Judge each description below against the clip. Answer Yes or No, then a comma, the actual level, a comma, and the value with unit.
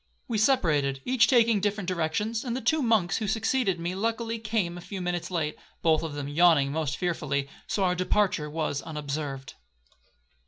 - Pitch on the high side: No, medium, 180 Hz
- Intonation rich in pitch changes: Yes, wide, 6.2 semitones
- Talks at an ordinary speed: Yes, average, 170 wpm